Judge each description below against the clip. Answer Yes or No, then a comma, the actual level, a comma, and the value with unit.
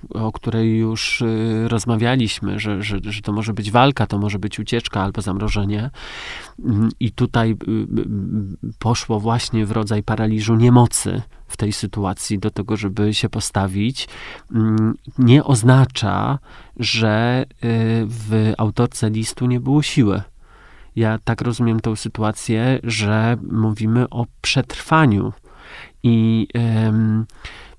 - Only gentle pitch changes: Yes, narrow, 2.0 semitones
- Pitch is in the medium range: No, low, 110 Hz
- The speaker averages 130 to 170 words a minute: No, slow, 110 wpm